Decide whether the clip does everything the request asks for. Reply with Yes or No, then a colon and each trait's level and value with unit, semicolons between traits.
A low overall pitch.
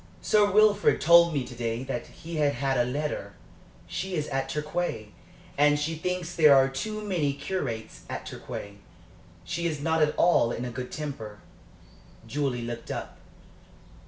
No: medium, 150 Hz